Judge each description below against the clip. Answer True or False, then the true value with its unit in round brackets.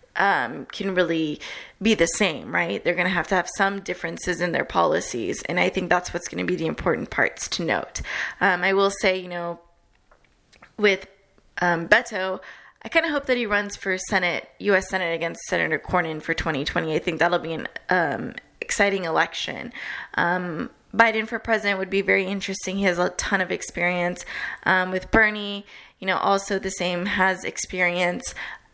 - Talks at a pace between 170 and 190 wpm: True (180 wpm)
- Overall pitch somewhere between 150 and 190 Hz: True (185 Hz)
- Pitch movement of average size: False (2.2 semitones)